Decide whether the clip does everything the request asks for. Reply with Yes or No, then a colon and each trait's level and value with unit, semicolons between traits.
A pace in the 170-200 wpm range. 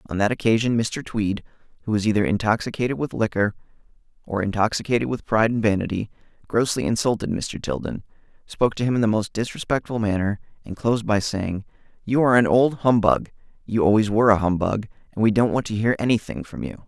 Yes: average, 185 wpm